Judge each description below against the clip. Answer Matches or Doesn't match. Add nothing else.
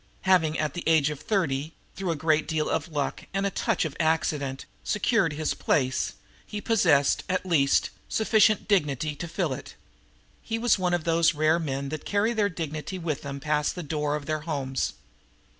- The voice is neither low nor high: Matches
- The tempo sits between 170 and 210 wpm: Matches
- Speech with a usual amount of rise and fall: Matches